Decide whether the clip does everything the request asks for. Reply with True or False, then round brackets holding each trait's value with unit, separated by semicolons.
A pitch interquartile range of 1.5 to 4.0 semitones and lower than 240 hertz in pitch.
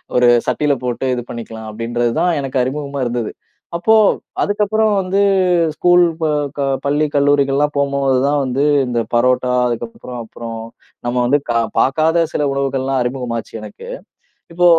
True (3.5 semitones; 135 Hz)